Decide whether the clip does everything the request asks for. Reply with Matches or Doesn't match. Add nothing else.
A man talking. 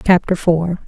Doesn't match